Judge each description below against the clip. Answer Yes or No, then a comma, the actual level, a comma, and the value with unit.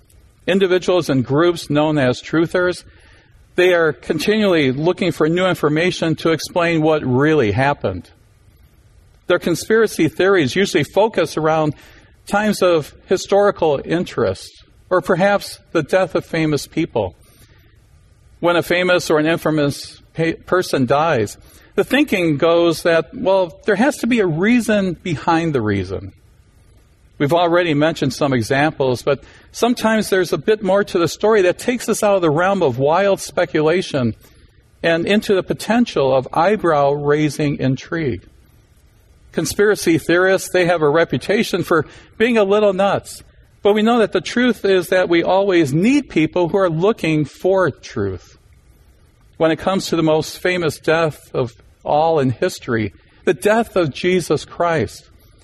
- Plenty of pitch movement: Yes, wide, 6.7 semitones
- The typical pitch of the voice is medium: Yes, medium, 165 Hz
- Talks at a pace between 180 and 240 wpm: No, average, 145 wpm